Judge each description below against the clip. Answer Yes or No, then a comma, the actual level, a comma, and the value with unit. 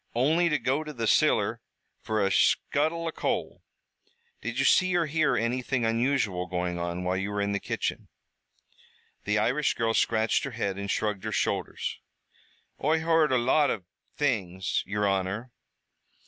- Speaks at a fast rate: No, average, 160 wpm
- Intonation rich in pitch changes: Yes, wide, 6.6 semitones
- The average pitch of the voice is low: Yes, low, 115 Hz